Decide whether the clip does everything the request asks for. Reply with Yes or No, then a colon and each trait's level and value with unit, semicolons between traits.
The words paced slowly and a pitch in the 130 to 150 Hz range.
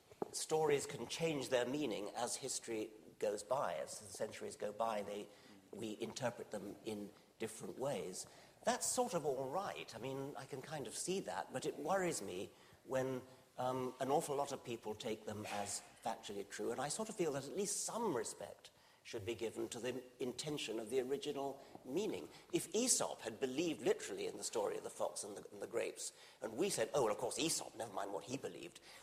No: fast, 205 wpm; medium, 140 Hz